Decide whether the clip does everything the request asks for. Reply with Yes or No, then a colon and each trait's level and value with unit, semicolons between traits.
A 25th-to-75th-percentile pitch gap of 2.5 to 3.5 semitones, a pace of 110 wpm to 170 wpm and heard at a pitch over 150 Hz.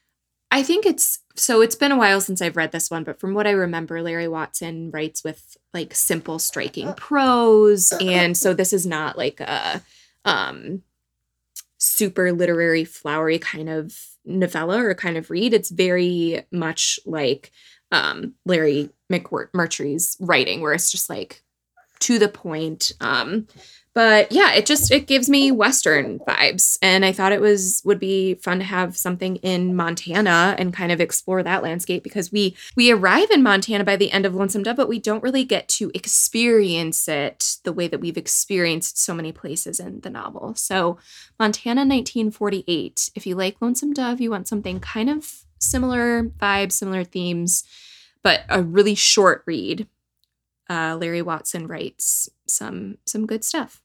No: average, 4.2 semitones; average, 165 wpm; medium, 185 Hz